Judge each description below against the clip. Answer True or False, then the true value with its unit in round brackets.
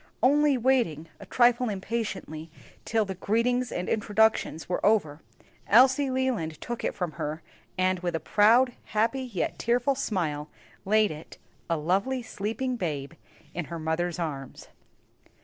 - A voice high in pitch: True (205 Hz)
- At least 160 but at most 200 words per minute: False (140 wpm)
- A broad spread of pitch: True (6.8 semitones)